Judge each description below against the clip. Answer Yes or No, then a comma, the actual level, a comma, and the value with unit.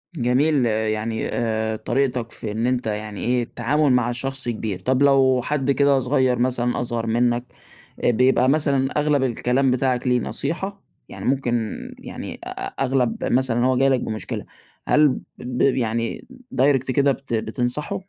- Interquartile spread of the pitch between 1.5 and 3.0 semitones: Yes, narrow, 2.4 semitones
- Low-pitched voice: Yes, low, 125 Hz